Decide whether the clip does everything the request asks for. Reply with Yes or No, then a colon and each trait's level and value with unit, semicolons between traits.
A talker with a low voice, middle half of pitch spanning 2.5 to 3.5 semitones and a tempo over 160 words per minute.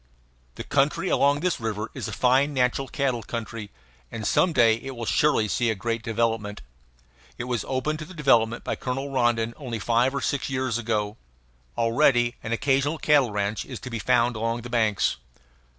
Yes: low, 120 Hz; average, 3.2 semitones; average, 180 wpm